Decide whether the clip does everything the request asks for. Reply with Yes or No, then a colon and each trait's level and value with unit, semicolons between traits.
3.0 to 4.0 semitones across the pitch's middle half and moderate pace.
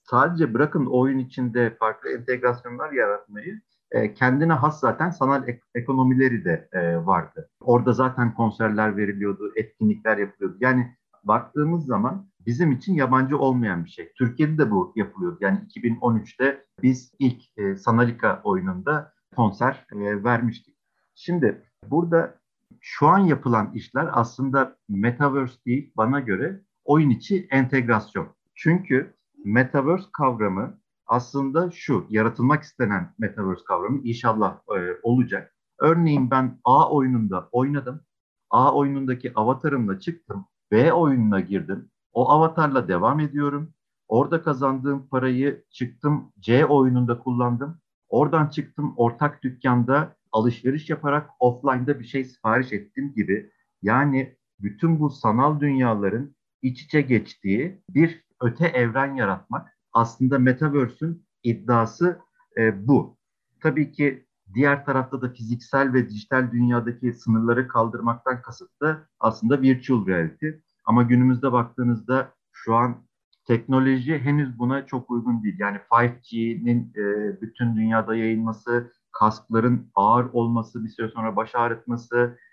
Yes: average, 3.7 semitones; average, 115 wpm